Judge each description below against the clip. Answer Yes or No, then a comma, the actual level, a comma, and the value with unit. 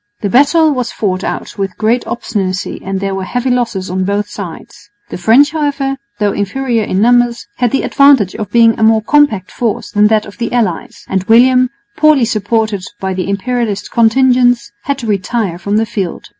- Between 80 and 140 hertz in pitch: No, high, 225 Hz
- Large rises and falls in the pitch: No, average, 3.8 semitones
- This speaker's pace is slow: No, average, 185 wpm